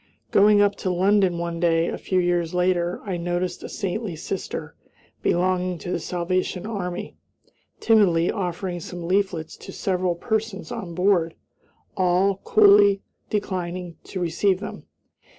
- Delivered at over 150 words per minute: No, slow, 135 wpm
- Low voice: No, medium, 185 Hz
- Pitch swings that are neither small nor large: No, narrow, 2.3 semitones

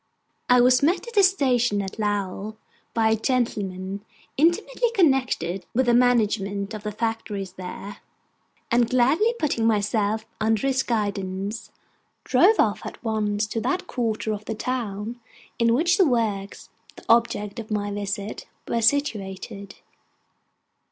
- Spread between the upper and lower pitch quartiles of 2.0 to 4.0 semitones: Yes, average, 3.6 semitones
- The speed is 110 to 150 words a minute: Yes, average, 140 wpm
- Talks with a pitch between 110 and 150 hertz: No, high, 220 Hz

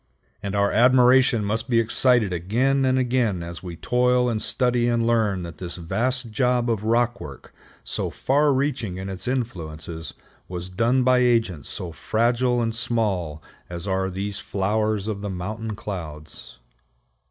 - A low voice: Yes, low, 110 Hz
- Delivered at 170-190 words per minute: No, average, 155 wpm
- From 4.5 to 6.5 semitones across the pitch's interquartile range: Yes, average, 4.9 semitones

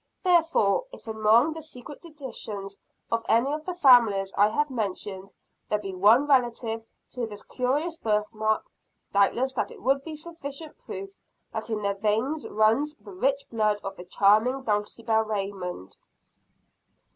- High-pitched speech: Yes, high, 225 Hz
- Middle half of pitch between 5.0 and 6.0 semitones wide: Yes, average, 5.3 semitones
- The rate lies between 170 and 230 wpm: No, average, 145 wpm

